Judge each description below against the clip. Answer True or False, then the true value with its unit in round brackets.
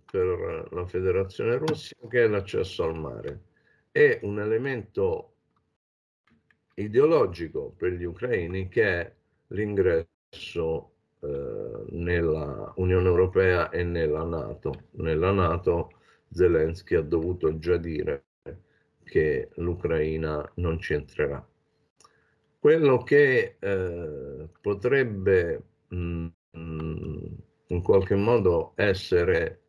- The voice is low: True (100 Hz)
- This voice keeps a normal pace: False (95 wpm)